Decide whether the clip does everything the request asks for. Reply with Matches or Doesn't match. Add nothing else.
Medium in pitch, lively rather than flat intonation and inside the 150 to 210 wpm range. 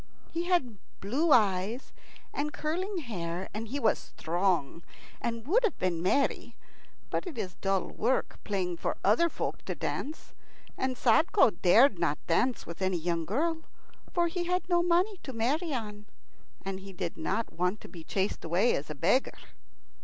Doesn't match